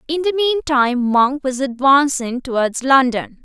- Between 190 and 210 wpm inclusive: No, average, 155 wpm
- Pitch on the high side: Yes, very high, 270 Hz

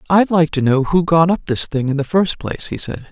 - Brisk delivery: Yes, fast, 290 wpm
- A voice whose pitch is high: No, medium, 155 Hz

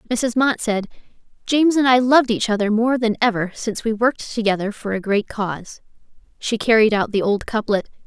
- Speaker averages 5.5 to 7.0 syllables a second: Yes, 5.7 syllables/s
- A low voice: No, high, 225 Hz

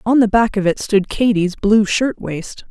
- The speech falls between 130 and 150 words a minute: No, average, 200 wpm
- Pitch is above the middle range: Yes, high, 210 Hz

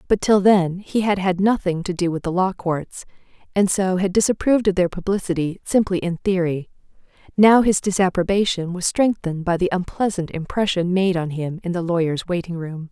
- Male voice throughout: No, female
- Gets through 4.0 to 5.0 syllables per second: No, 5.3 syllables/s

